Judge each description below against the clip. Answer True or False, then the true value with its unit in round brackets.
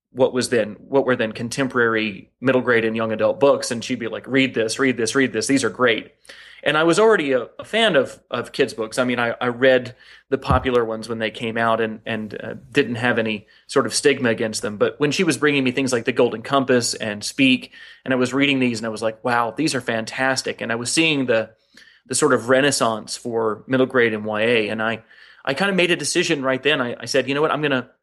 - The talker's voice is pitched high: False (125 Hz)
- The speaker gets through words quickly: True (255 wpm)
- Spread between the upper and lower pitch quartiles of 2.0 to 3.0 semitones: False (3.4 semitones)